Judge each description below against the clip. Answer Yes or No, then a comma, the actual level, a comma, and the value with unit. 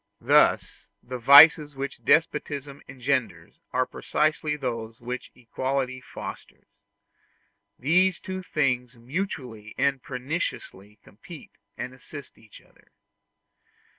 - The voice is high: No, low, 135 Hz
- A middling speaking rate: No, slow, 100 wpm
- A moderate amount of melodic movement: Yes, average, 3.4 semitones